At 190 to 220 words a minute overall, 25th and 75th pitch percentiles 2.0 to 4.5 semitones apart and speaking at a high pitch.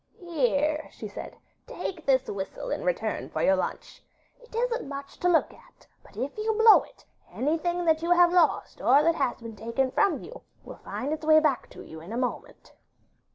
No: average, 200 wpm; average, 5.3 semitones; very high, 310 Hz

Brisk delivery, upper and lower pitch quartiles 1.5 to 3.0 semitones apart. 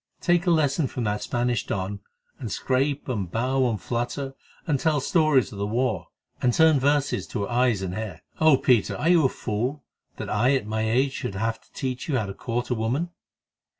No: fast, 210 wpm; average, 4.2 semitones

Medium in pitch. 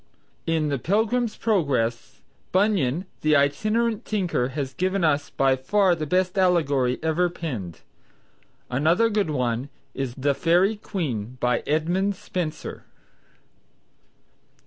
Yes: medium, 160 Hz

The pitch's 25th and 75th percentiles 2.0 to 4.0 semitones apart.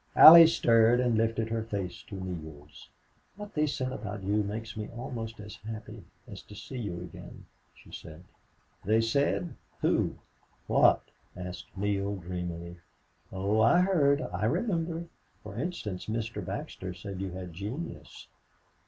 No: average, 4.7 semitones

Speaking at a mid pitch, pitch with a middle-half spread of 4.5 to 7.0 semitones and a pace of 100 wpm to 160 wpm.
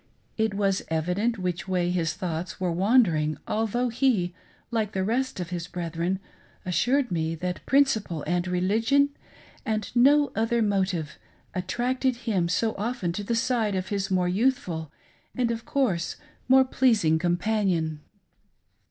No: high, 195 Hz; average, 5.0 semitones; average, 150 wpm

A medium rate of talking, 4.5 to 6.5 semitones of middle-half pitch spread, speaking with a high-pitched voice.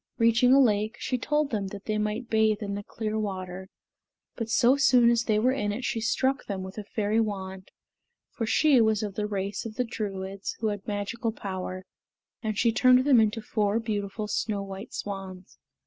No: average, 195 wpm; narrow, 2.5 semitones; high, 215 Hz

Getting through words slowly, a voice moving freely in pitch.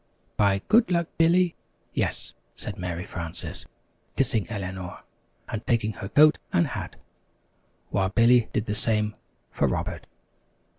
Yes: slow, 130 wpm; wide, 6.8 semitones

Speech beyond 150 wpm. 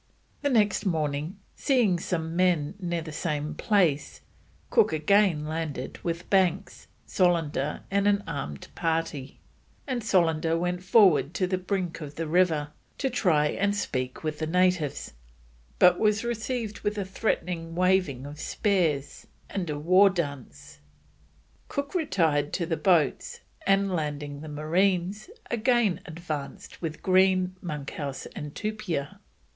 No: slow, 135 wpm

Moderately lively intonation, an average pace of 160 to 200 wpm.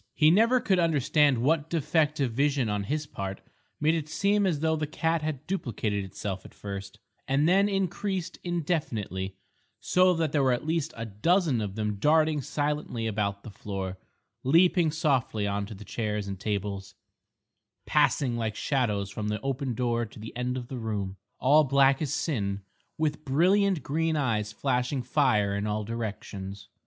No: wide, 6.9 semitones; average, 165 wpm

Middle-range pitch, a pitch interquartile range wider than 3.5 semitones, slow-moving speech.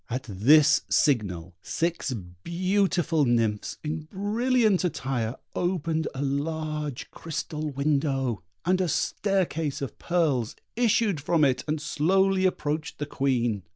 Yes: medium, 150 Hz; average, 4.7 semitones; slow, 120 wpm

